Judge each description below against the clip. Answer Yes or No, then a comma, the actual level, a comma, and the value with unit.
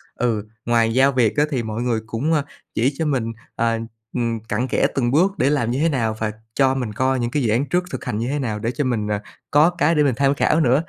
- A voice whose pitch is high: No, low, 125 Hz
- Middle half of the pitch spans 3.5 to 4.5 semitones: Yes, average, 3.9 semitones